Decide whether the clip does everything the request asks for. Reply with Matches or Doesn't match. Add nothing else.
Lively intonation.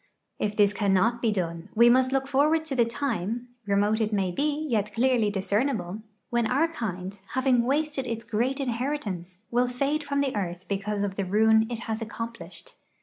Doesn't match